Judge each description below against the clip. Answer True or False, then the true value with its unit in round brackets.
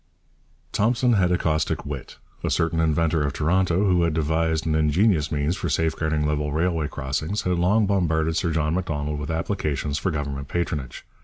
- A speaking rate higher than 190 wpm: False (170 wpm)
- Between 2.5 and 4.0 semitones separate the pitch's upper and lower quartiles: True (2.9 semitones)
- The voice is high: False (80 Hz)